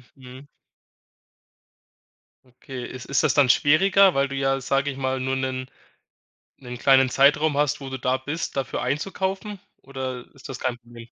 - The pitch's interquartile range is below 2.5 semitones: Yes, narrow, 1.9 semitones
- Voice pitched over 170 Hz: No, low, 135 Hz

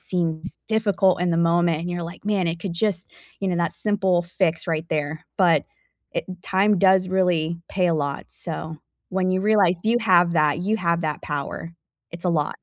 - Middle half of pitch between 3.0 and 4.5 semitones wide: No, narrow, 2.4 semitones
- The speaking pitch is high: No, medium, 175 Hz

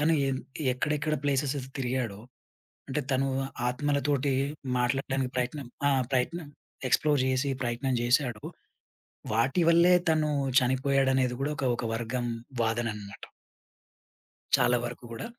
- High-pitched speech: No, low, 130 Hz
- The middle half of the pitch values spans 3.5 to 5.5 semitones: No, average, 2.7 semitones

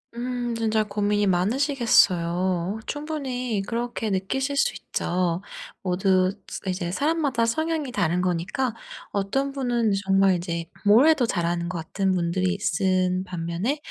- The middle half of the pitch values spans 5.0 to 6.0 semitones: Yes, wide, 5.4 semitones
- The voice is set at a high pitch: Yes, high, 200 Hz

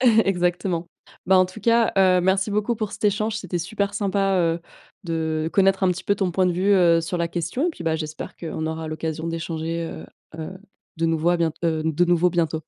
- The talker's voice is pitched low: No, medium, 175 Hz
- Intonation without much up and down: No, average, 3.0 semitones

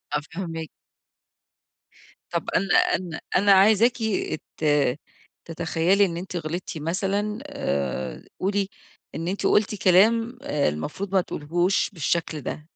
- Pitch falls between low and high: Yes, medium, 180 Hz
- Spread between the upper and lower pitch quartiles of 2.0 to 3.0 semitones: No, average, 3.7 semitones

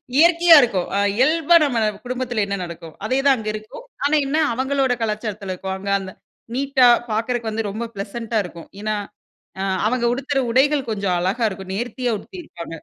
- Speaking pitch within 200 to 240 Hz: Yes, high, 230 Hz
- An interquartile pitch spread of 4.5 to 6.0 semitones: Yes, average, 5.1 semitones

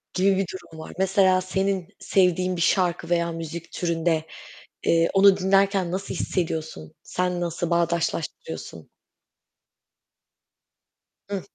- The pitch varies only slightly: Yes, narrow, 2.2 semitones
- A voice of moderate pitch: Yes, medium, 180 Hz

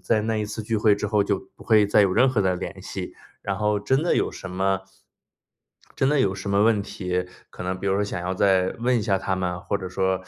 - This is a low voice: Yes, low, 100 Hz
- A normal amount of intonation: No, narrow, 2.3 semitones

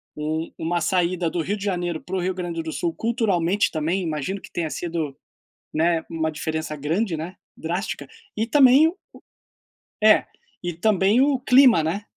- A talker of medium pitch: Yes, medium, 175 Hz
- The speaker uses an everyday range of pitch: Yes, average, 3.8 semitones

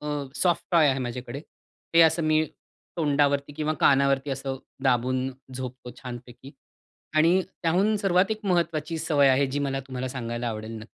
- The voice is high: No, medium, 140 Hz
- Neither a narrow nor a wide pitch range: Yes, average, 3.7 semitones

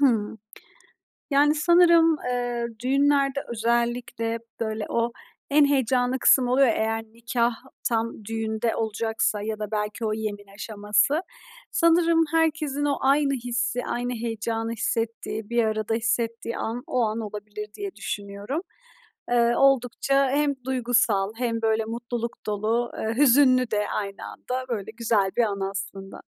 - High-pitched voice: Yes, high, 235 Hz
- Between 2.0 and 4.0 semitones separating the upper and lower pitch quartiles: Yes, average, 3.1 semitones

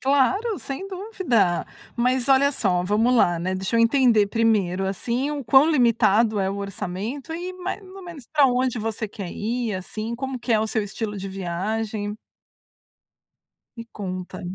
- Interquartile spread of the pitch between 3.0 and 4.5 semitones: No, average, 5.0 semitones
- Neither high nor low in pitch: No, high, 230 Hz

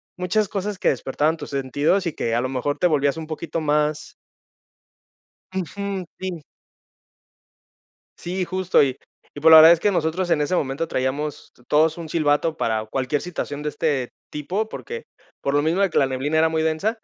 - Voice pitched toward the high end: No, medium, 155 Hz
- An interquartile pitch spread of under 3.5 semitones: No, average, 3.9 semitones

